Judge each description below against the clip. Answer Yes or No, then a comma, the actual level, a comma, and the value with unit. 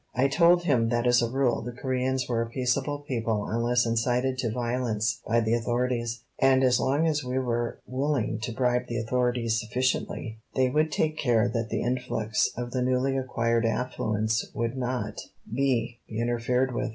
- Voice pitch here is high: No, low, 125 Hz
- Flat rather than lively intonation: Yes, narrow, 1.9 semitones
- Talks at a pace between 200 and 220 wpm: No, average, 175 wpm